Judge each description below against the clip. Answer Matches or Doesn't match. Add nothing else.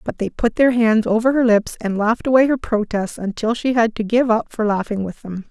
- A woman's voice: Matches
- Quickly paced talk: Matches